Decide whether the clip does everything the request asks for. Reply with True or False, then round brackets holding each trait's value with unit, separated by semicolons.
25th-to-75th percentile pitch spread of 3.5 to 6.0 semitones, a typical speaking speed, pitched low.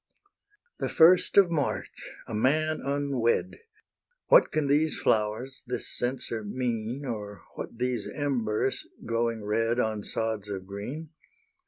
False (4.7 semitones; 125 wpm; 120 Hz)